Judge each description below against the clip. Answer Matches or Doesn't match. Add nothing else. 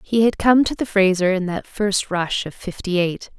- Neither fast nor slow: Doesn't match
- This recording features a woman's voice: Matches